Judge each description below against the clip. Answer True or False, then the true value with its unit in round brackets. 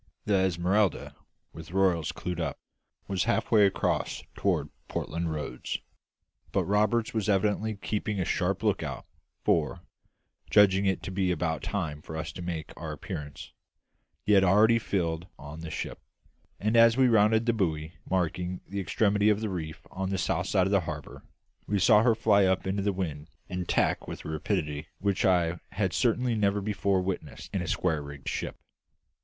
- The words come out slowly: False (170 wpm)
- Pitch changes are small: False (3.8 semitones)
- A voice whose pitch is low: True (95 Hz)